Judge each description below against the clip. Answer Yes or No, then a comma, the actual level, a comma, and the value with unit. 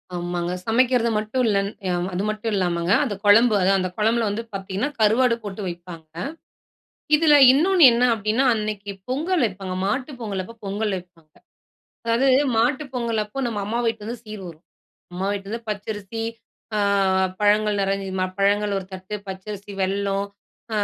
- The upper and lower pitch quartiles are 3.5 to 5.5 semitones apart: No, average, 3.1 semitones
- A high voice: Yes, high, 210 Hz